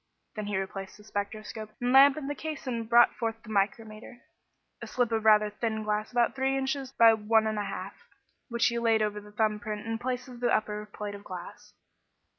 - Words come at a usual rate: No, fast, 220 wpm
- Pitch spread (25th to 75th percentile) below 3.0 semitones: Yes, narrow, 2.4 semitones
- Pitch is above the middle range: Yes, high, 220 Hz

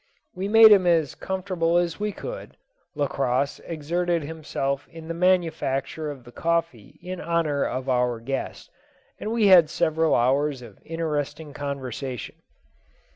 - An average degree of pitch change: Yes, average, 4.1 semitones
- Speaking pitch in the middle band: Yes, medium, 160 Hz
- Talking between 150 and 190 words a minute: No, slow, 135 wpm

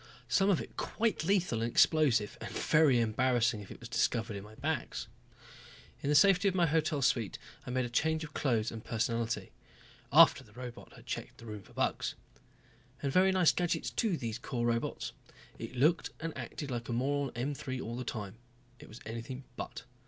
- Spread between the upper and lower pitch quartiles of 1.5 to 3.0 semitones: No, average, 5.1 semitones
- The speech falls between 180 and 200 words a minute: Yes, average, 195 wpm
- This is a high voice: No, low, 125 Hz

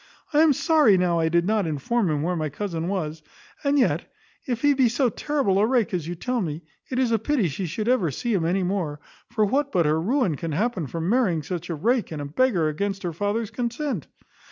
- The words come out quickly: Yes, fast, 225 wpm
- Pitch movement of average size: No, wide, 6.6 semitones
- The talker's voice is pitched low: No, high, 195 Hz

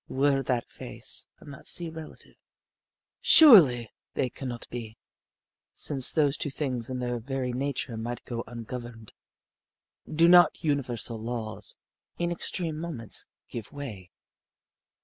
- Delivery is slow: Yes, slow, 130 wpm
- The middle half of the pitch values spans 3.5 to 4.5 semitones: Yes, average, 3.8 semitones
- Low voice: Yes, low, 130 Hz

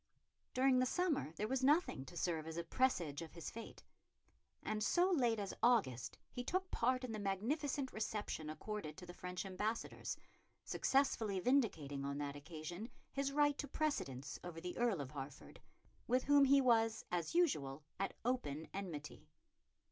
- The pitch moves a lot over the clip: Yes, wide, 8.3 semitones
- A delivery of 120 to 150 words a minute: No, average, 165 wpm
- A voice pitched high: Yes, high, 210 Hz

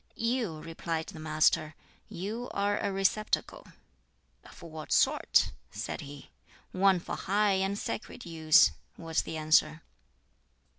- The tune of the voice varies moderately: Yes, average, 4.3 semitones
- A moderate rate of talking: No, slow, 120 wpm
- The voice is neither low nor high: Yes, medium, 170 Hz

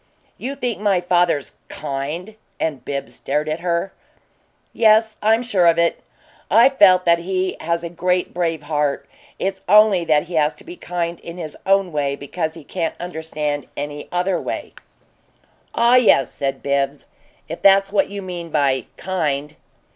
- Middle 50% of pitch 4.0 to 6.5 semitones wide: Yes, average, 4.4 semitones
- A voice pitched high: No, medium, 170 Hz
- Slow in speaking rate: No, average, 160 wpm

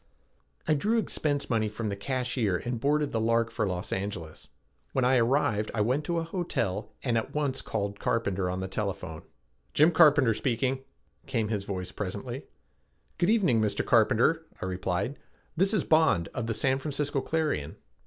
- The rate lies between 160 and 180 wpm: Yes, average, 170 wpm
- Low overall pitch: Yes, low, 115 Hz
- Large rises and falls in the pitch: Yes, wide, 6.1 semitones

